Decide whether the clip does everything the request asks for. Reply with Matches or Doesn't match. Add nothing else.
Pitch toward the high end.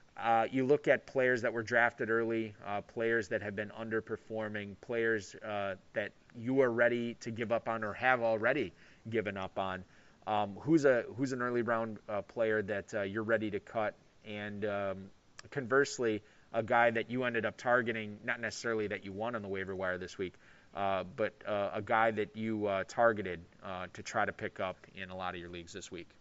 Doesn't match